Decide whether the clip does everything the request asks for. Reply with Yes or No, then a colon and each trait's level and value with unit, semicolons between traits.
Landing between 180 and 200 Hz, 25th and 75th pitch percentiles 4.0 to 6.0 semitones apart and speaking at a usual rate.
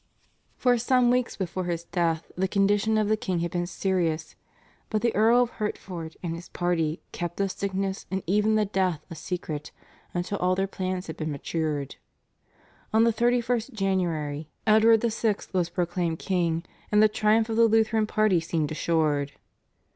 Yes: high, 190 Hz; average, 4.4 semitones; average, 170 wpm